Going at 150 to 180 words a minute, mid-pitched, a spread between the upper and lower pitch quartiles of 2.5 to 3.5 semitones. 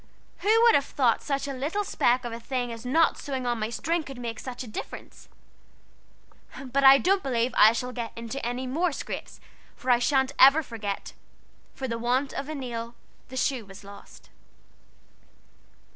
No: average, 175 wpm; very high, 255 Hz; average, 2.9 semitones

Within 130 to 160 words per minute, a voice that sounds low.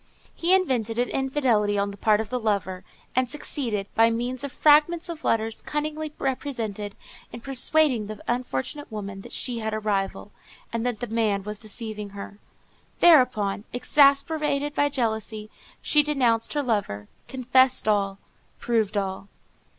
No: average, 150 wpm; high, 230 Hz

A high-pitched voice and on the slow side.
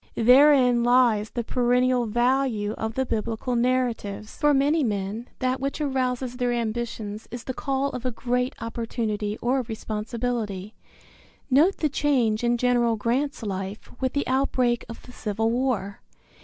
No: high, 240 Hz; average, 145 wpm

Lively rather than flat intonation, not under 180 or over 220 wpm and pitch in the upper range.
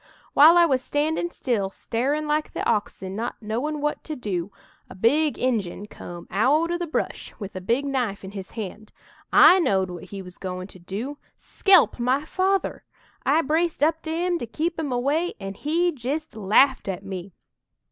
Yes: wide, 7.7 semitones; average, 185 wpm; very high, 255 Hz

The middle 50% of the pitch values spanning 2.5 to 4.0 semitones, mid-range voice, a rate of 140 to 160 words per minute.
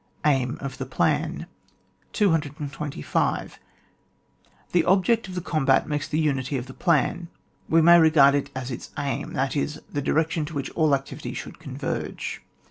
Yes: average, 3.1 semitones; medium, 145 Hz; average, 155 wpm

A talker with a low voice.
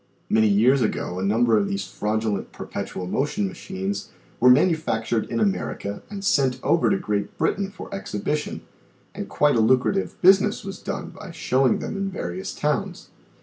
Yes: low, 130 Hz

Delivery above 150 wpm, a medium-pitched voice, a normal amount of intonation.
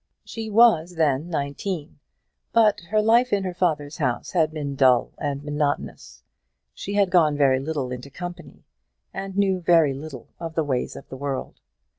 Yes: average, 165 wpm; medium, 155 Hz; average, 5.0 semitones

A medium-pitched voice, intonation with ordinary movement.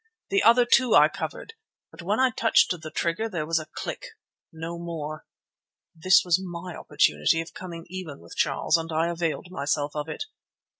Yes: medium, 170 Hz; average, 3.0 semitones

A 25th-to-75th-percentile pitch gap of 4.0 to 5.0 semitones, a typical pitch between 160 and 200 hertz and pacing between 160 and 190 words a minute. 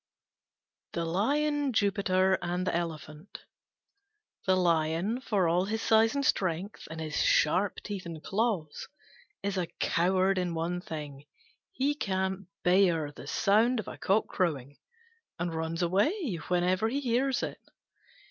No: average, 4.4 semitones; medium, 185 Hz; average, 140 wpm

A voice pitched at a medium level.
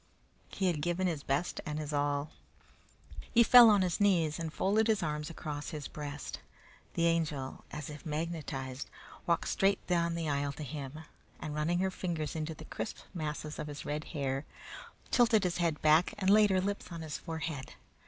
Yes: medium, 160 Hz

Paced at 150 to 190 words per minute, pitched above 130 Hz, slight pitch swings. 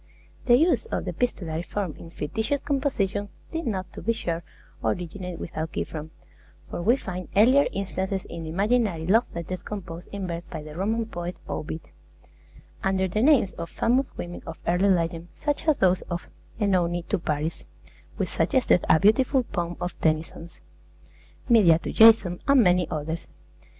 No: average, 160 wpm; medium, 185 Hz; average, 4.8 semitones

